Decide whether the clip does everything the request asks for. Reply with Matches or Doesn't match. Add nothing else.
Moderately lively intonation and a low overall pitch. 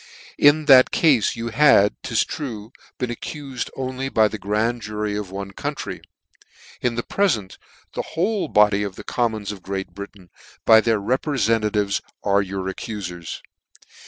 Matches